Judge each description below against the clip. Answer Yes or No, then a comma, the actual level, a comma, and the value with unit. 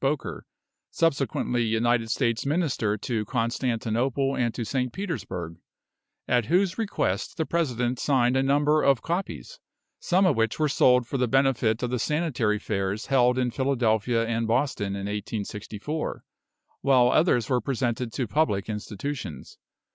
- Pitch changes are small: No, average, 3.7 semitones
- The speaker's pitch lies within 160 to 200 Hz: No, low, 125 Hz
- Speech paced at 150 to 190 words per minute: No, average, 140 wpm